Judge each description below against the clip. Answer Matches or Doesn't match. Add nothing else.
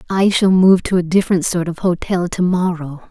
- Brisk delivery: Matches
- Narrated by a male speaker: Doesn't match